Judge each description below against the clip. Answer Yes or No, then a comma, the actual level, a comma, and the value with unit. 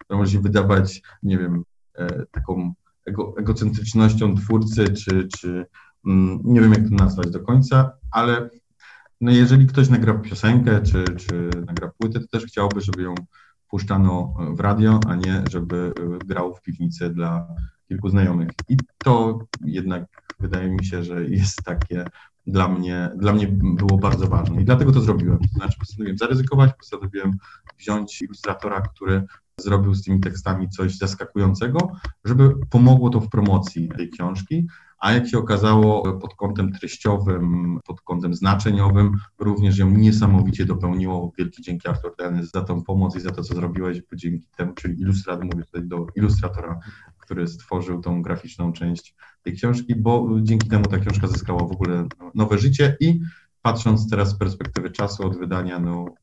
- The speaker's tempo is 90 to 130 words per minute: No, average, 155 wpm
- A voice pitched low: Yes, very low, 95 Hz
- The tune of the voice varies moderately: Yes, average, 3.4 semitones